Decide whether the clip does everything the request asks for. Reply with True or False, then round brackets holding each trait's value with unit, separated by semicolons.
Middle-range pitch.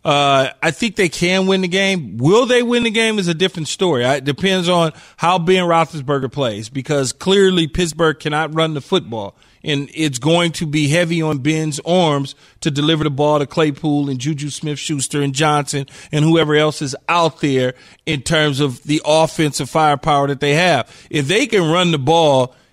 True (155 Hz)